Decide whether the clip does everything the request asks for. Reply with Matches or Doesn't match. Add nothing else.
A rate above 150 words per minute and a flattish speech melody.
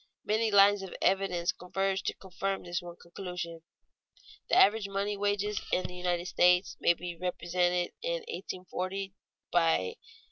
Doesn't match